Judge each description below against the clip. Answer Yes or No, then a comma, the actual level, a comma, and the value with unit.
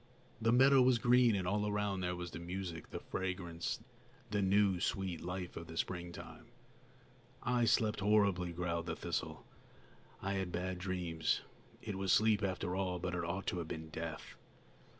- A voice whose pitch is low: Yes, very low, 95 Hz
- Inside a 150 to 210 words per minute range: Yes, average, 170 wpm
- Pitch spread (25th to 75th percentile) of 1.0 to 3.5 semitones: Yes, average, 2.9 semitones